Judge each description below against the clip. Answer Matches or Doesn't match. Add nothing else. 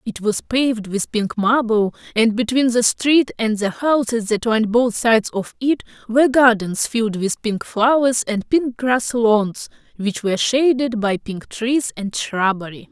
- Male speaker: Doesn't match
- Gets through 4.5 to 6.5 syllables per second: Doesn't match